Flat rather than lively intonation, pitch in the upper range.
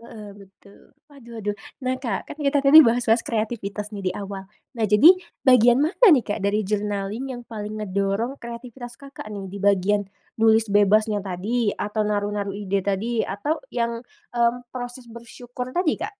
No: average, 3.2 semitones; high, 220 Hz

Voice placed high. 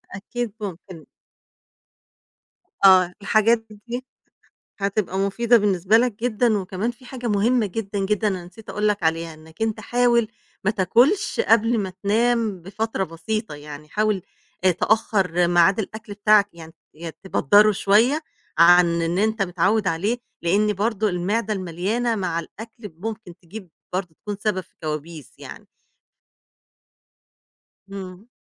Yes: high, 200 Hz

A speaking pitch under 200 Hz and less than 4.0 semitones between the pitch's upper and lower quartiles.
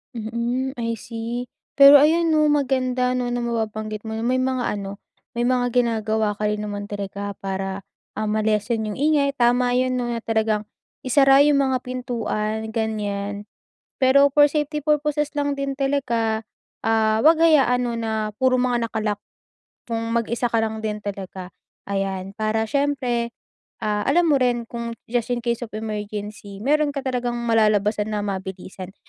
No: high, 230 Hz; average, 3.3 semitones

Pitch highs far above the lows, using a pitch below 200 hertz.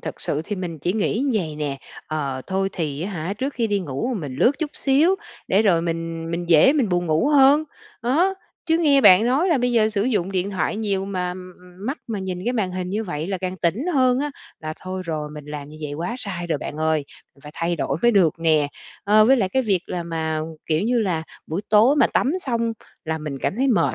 Yes: wide, 6.6 semitones; high, 190 Hz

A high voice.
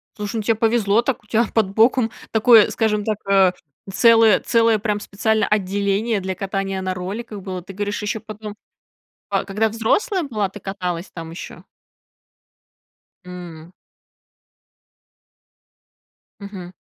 Yes: high, 205 Hz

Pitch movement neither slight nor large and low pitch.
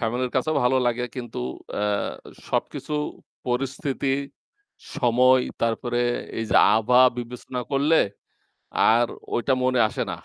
No: narrow, 1.7 semitones; low, 125 Hz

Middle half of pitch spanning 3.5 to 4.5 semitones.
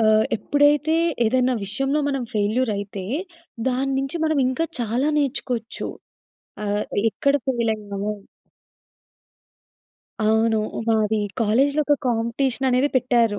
Yes: average, 3.8 semitones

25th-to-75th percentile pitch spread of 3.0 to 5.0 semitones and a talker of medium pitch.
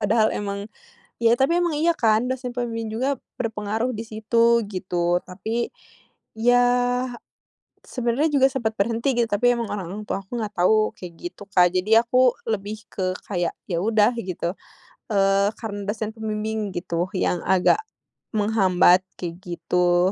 No: average, 3.7 semitones; high, 215 Hz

